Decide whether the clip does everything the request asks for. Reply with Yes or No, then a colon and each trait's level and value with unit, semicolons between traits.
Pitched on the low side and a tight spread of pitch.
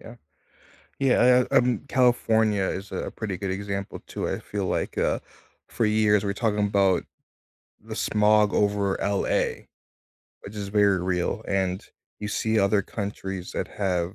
Yes: low, 100 Hz; narrow, 1.8 semitones